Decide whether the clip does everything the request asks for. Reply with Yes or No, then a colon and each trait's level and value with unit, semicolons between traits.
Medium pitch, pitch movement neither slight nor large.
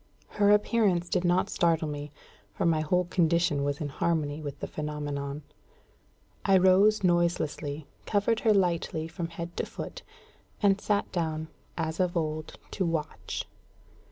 Yes: medium, 170 Hz; average, 3.2 semitones